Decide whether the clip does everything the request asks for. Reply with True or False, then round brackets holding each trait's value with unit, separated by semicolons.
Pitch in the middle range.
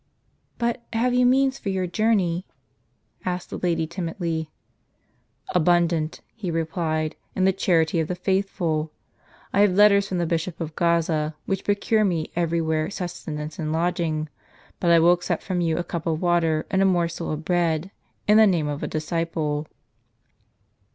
True (170 Hz)